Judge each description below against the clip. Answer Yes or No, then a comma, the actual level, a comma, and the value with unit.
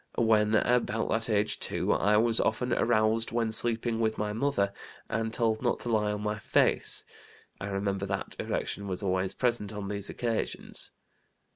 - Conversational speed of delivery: Yes, average, 165 wpm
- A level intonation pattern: Yes, narrow, 1.9 semitones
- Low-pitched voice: Yes, low, 110 Hz